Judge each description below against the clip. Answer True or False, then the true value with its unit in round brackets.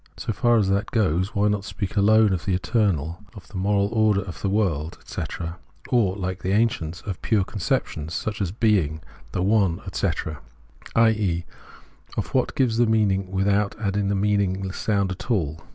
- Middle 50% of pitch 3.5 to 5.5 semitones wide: False (2.7 semitones)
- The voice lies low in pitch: True (100 Hz)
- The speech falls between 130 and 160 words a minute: False (180 wpm)